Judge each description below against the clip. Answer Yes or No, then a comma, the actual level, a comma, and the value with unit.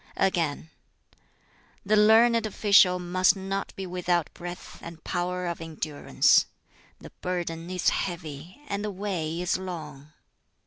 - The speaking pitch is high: No, medium, 180 Hz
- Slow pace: Yes, slow, 125 wpm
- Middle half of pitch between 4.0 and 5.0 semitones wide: No, average, 2.7 semitones